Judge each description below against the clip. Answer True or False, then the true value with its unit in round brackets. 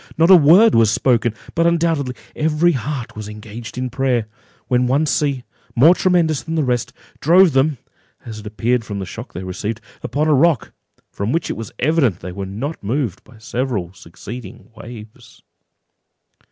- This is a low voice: True (125 Hz)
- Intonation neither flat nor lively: False (6.0 semitones)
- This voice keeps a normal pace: True (170 wpm)